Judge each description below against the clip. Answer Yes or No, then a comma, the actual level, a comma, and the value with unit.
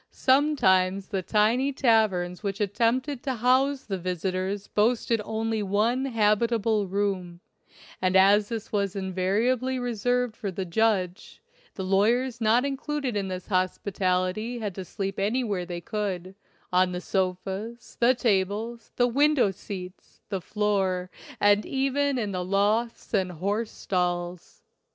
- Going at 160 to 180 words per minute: No, slow, 135 wpm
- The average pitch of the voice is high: Yes, high, 205 Hz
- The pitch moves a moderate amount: Yes, average, 4.1 semitones